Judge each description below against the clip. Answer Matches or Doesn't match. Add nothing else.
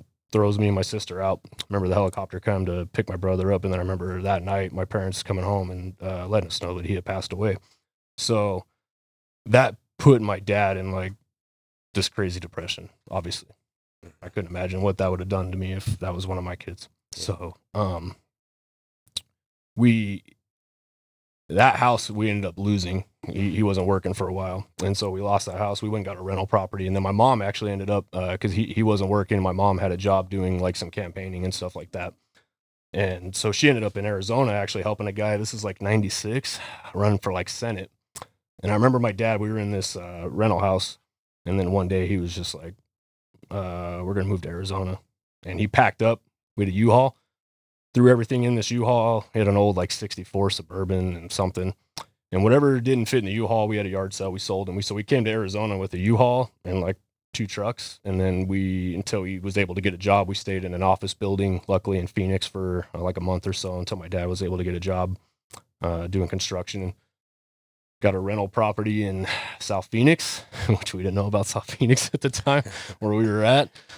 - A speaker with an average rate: Doesn't match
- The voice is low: Matches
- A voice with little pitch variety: Matches